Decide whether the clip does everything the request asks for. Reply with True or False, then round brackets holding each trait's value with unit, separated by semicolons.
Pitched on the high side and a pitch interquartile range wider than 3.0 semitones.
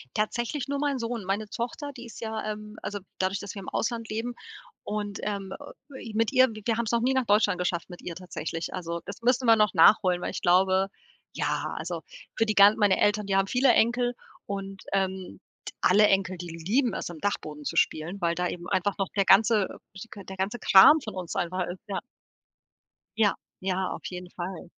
True (200 Hz; 3.5 semitones)